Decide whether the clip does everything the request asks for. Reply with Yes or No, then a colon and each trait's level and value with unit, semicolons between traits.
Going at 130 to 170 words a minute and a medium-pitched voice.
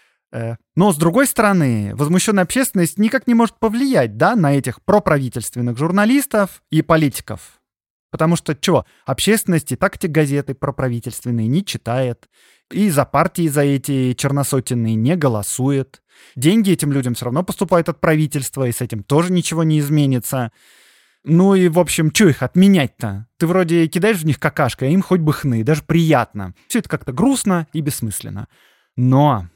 Yes: fast, 160 wpm; medium, 150 Hz